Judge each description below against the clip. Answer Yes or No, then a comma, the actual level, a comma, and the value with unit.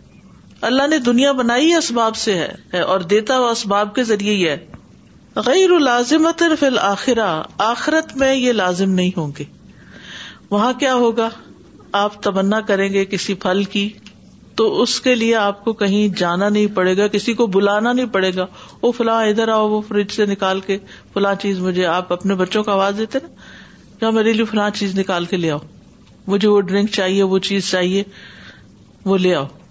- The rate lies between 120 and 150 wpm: No, average, 180 wpm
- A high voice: Yes, high, 205 Hz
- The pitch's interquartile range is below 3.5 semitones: Yes, average, 3.0 semitones